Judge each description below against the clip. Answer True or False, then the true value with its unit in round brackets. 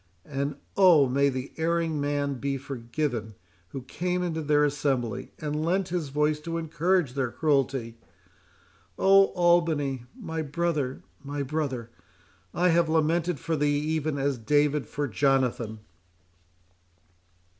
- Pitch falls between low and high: True (145 Hz)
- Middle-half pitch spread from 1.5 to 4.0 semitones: True (3.3 semitones)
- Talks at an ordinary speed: False (125 wpm)